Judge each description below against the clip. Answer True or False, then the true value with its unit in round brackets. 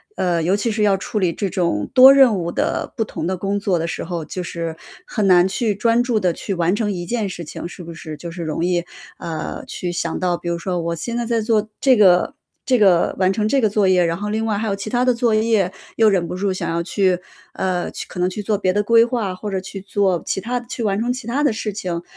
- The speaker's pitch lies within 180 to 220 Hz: True (195 Hz)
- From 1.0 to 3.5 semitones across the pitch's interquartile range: False (3.9 semitones)